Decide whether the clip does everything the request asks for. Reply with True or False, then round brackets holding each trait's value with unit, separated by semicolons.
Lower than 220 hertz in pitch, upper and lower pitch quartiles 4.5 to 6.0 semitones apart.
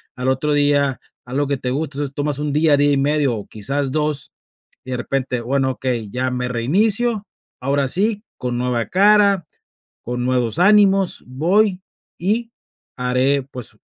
True (140 Hz; 5.3 semitones)